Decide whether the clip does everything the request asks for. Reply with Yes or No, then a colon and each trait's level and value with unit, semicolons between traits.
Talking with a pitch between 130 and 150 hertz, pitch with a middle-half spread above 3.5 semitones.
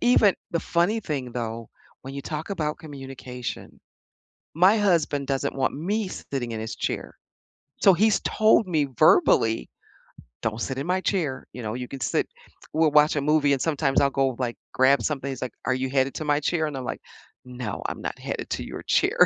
Yes: medium, 140 Hz; average, 3.9 semitones